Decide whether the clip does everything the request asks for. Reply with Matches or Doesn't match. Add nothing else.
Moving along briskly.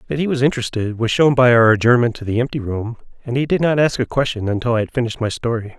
Matches